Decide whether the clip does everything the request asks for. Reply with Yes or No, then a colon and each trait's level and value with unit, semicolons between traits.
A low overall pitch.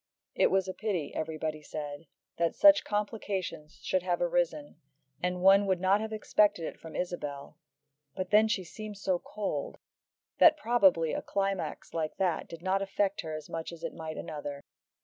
No: medium, 180 Hz